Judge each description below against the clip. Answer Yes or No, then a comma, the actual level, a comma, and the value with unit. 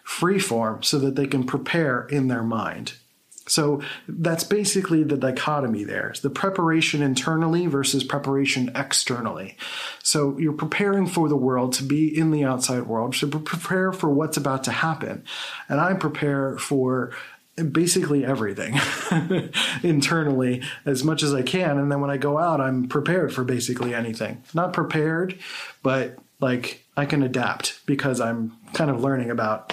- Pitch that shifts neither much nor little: Yes, average, 3.8 semitones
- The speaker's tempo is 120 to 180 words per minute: Yes, average, 160 wpm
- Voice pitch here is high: No, medium, 140 Hz